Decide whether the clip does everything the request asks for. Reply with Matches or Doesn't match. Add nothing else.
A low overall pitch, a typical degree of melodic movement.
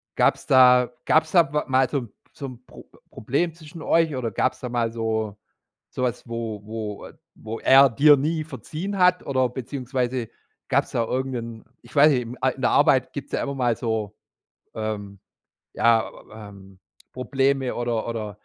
Matches